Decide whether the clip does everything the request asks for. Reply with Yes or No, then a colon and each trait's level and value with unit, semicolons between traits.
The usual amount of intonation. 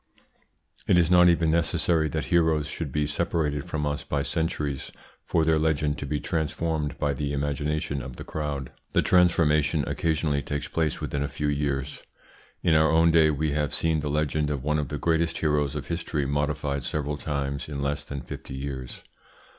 No: narrow, 1.9 semitones